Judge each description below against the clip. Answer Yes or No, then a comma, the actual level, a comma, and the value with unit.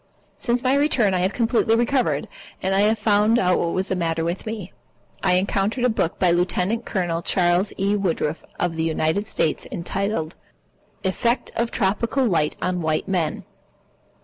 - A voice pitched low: No, high, 190 Hz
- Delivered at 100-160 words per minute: No, average, 175 wpm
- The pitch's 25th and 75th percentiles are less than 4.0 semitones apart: No, average, 4.4 semitones